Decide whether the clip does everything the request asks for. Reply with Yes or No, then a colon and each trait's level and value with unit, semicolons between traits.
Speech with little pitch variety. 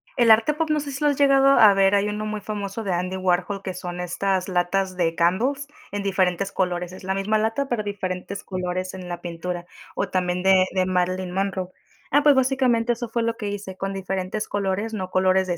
No: average, 3.2 semitones